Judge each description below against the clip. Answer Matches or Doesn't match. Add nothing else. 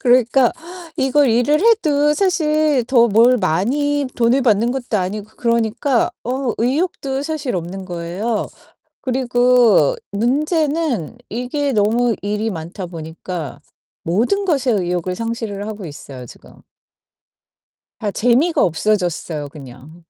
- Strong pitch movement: Matches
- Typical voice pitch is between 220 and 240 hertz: Matches